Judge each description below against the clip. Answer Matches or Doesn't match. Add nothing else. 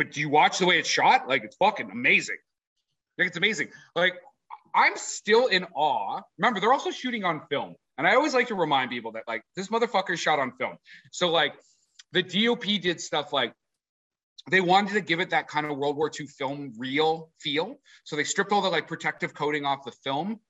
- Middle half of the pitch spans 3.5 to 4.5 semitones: Doesn't match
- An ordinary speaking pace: Doesn't match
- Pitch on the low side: Doesn't match